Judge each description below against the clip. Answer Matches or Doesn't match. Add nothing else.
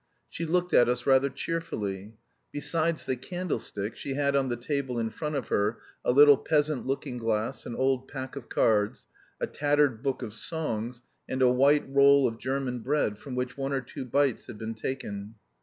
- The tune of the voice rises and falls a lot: Doesn't match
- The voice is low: Matches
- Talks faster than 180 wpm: Matches